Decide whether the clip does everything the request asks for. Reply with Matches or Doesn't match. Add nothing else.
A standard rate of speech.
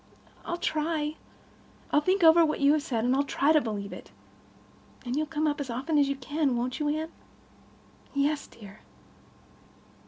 Matches